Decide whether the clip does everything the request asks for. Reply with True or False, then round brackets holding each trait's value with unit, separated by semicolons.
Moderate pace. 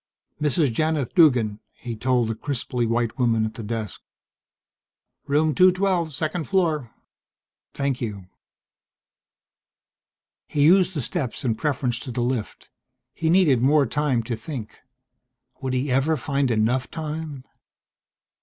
False (125 wpm)